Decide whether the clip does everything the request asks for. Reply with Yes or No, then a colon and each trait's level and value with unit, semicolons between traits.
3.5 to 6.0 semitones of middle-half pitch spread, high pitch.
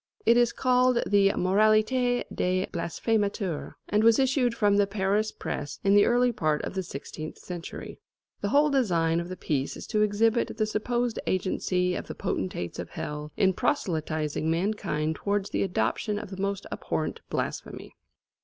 Yes: average, 4.5 semitones; high, 200 Hz